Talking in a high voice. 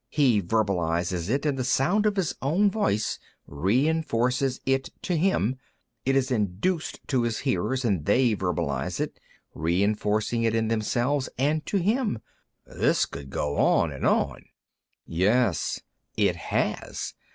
No: low, 120 Hz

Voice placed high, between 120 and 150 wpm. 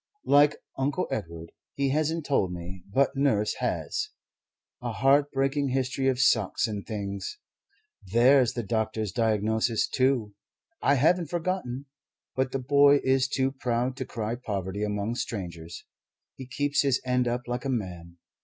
No: low, 125 Hz; average, 145 wpm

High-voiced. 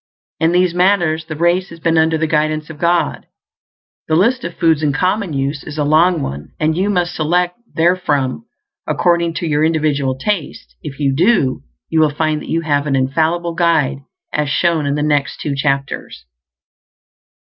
No: medium, 160 Hz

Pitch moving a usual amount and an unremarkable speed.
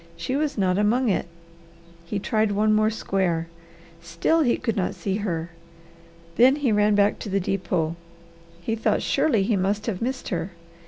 Yes: average, 3.3 semitones; average, 170 wpm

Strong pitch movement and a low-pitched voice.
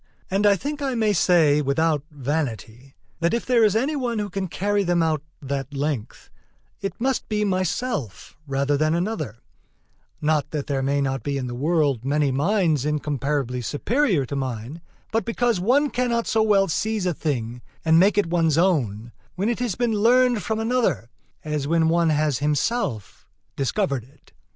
No: wide, 7.2 semitones; medium, 160 Hz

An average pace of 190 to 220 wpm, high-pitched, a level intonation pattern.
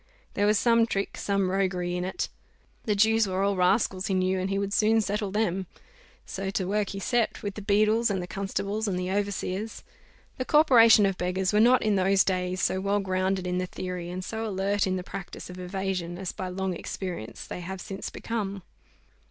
Yes: fast, 205 wpm; high, 195 Hz; narrow, 2.0 semitones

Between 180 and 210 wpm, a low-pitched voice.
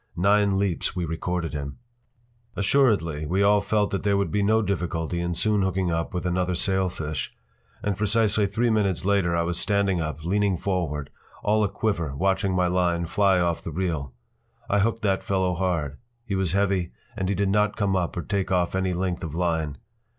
Yes: average, 185 wpm; very low, 95 Hz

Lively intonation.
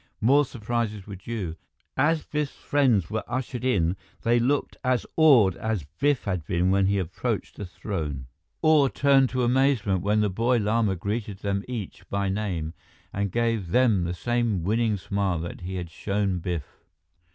No: average, 4.6 semitones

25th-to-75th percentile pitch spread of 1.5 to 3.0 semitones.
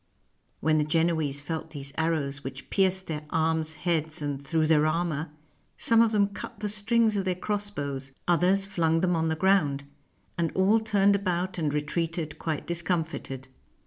No: average, 3.9 semitones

